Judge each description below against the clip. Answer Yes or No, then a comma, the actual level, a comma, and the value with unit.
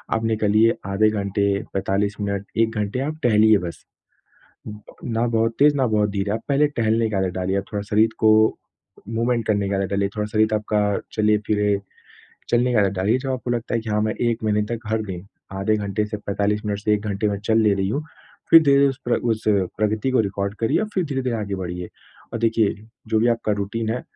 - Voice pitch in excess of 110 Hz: No, low, 105 Hz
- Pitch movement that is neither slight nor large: No, narrow, 2.2 semitones